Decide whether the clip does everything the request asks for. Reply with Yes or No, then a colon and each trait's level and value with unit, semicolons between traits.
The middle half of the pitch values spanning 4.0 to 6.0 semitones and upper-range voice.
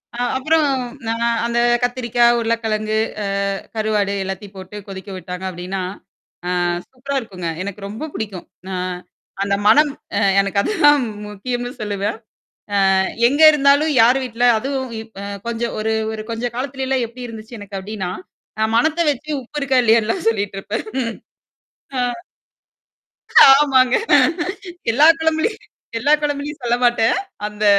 Yes: average, 4.5 semitones; high, 230 Hz